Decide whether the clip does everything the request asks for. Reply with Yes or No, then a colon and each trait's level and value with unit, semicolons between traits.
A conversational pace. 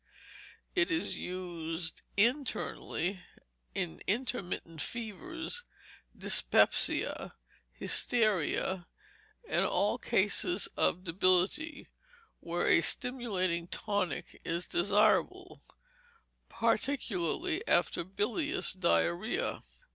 No: slow, 70 wpm